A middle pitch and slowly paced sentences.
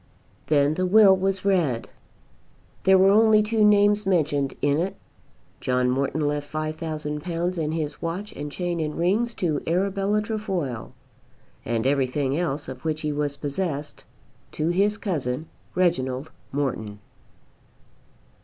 Yes: medium, 160 Hz; slow, 130 wpm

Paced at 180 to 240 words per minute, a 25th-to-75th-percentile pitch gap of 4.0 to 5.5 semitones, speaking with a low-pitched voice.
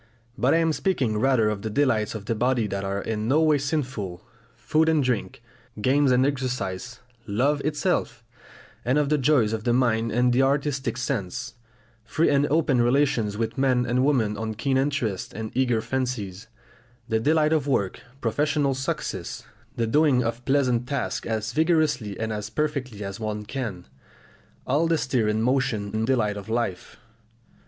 No: average, 170 wpm; average, 4.3 semitones; low, 125 Hz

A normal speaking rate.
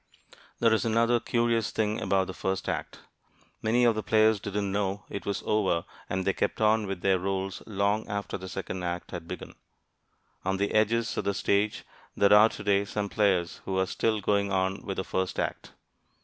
Yes: average, 190 wpm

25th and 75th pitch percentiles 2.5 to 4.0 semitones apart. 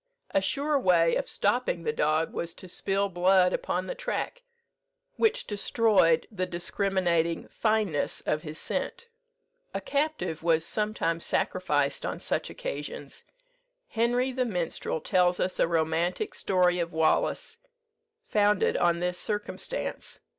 No: average, 4.6 semitones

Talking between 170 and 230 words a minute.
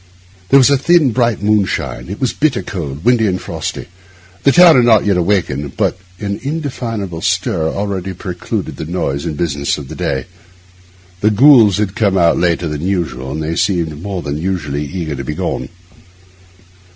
Yes: average, 175 wpm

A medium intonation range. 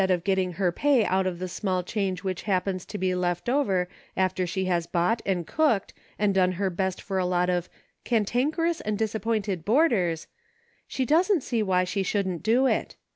Yes: average, 3.4 semitones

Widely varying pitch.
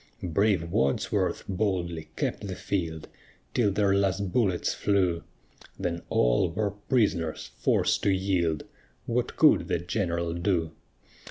No: average, 2.9 semitones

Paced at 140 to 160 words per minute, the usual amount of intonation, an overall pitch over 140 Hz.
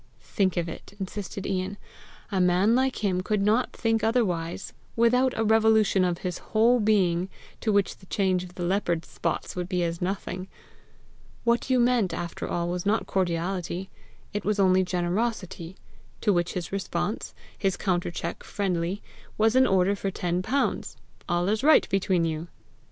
Yes: average, 155 wpm; average, 3.5 semitones; high, 190 Hz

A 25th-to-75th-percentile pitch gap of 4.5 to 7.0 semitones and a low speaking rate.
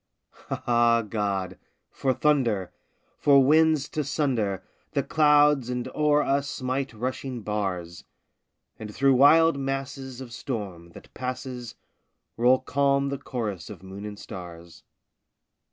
Yes: average, 4.9 semitones; slow, 120 wpm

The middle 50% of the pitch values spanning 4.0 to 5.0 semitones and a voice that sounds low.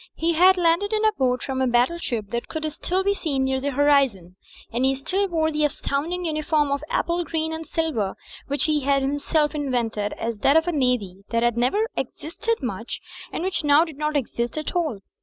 No: average, 4.7 semitones; very high, 290 Hz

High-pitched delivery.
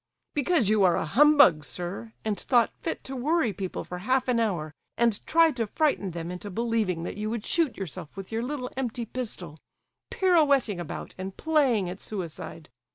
Yes: high, 225 Hz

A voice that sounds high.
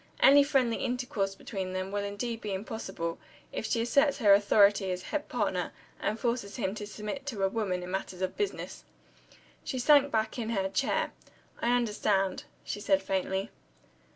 Yes: high, 210 Hz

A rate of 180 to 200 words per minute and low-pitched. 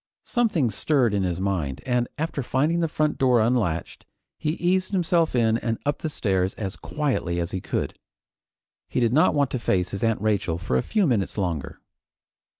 Yes: average, 185 wpm; low, 120 Hz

